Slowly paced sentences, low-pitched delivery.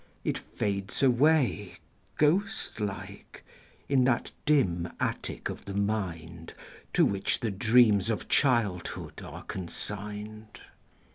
Yes: slow, 110 wpm; low, 105 Hz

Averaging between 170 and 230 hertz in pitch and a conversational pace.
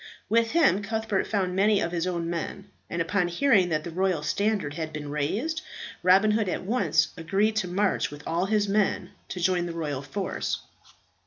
Yes: medium, 185 Hz; average, 185 wpm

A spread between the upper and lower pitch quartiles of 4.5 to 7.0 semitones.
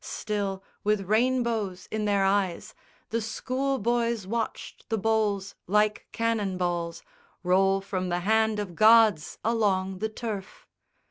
No: average, 2.7 semitones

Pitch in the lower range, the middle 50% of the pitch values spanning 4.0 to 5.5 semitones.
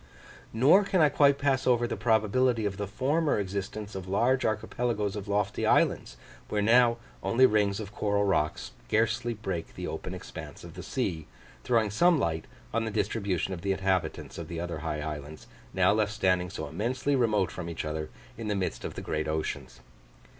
Yes: low, 105 Hz; average, 4.3 semitones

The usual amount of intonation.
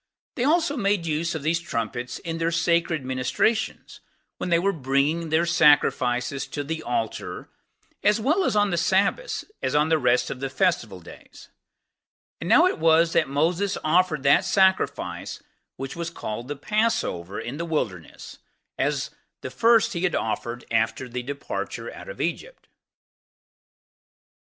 No: wide, 6.0 semitones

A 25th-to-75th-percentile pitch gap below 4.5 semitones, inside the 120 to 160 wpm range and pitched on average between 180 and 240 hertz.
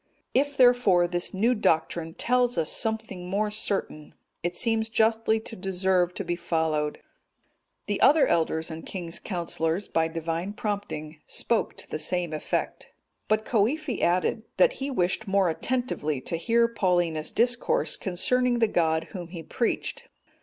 No: average, 5.2 semitones; average, 145 wpm; high, 190 Hz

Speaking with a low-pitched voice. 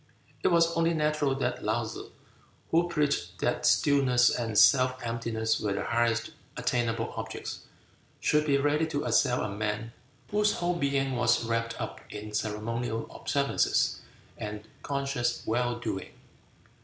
Yes: low, 120 Hz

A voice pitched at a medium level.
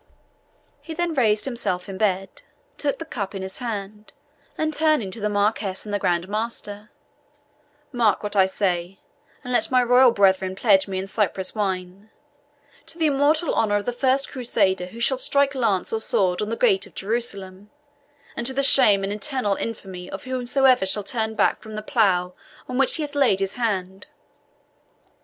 No: high, 210 Hz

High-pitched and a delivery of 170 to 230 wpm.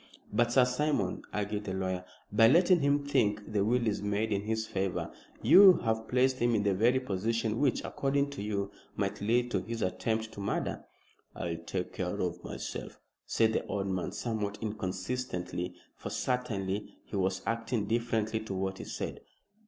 No: low, 110 Hz; average, 175 wpm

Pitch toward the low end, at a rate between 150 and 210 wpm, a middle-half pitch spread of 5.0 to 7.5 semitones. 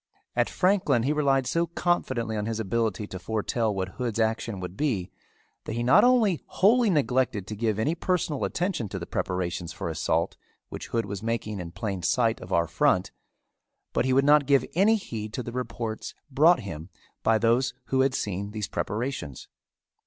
Yes: low, 115 Hz; average, 180 wpm; average, 5.3 semitones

